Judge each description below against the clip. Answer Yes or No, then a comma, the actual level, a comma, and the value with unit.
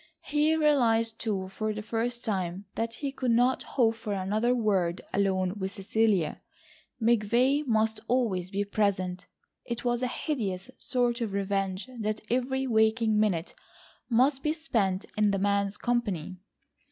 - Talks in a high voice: Yes, high, 220 Hz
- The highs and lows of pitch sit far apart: No, average, 3.6 semitones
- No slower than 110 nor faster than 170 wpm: Yes, average, 145 wpm